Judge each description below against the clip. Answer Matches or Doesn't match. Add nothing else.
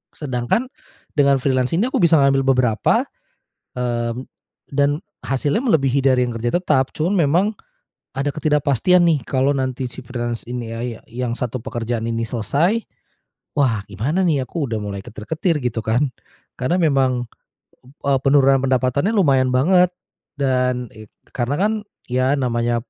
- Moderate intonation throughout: Matches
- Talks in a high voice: Doesn't match